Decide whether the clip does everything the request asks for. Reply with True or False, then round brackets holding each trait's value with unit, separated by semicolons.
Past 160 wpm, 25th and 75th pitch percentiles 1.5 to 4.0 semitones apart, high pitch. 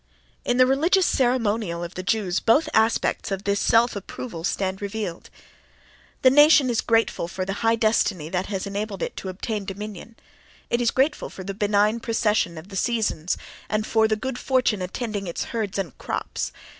True (180 wpm; 3.4 semitones; 215 Hz)